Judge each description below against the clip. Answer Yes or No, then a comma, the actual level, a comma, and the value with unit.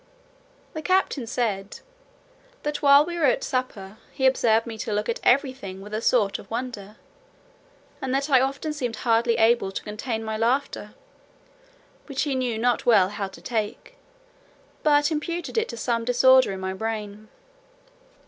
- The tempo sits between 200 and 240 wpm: No, average, 165 wpm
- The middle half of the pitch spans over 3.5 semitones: Yes, average, 4.1 semitones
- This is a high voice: Yes, high, 235 Hz